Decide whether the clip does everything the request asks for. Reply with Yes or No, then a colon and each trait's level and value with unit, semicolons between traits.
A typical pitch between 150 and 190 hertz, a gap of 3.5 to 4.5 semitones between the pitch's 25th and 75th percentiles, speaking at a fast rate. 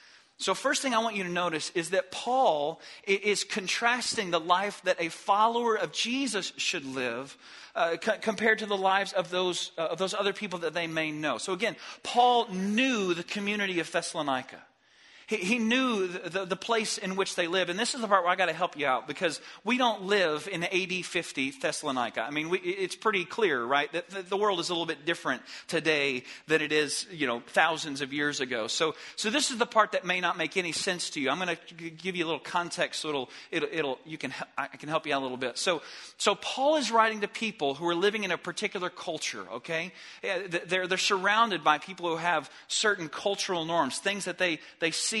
Yes: medium, 185 Hz; average, 4.2 semitones; fast, 220 wpm